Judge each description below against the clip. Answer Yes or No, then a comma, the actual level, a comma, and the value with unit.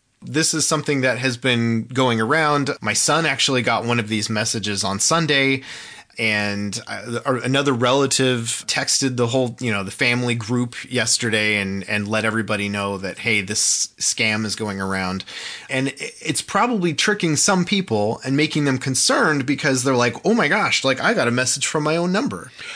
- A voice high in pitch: No, low, 125 Hz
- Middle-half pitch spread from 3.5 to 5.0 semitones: Yes, average, 4.5 semitones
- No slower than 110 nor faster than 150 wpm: No, average, 175 wpm